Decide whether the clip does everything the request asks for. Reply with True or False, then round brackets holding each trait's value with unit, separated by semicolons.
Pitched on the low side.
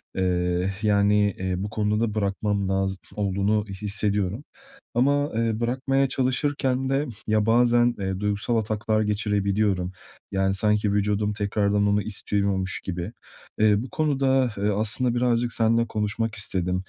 True (105 Hz)